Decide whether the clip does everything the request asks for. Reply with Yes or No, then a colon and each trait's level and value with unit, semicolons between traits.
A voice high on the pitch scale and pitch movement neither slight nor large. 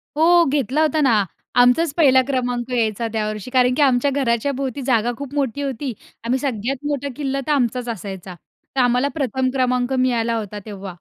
Yes: very high, 255 Hz; average, 3.1 semitones